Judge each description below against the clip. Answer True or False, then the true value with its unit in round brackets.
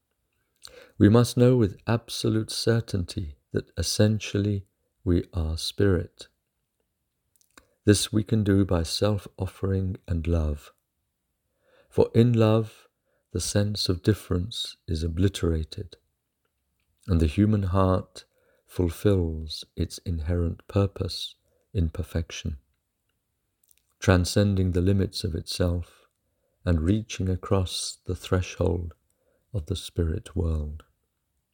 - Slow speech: True (100 wpm)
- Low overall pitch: True (95 Hz)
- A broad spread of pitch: False (3.4 semitones)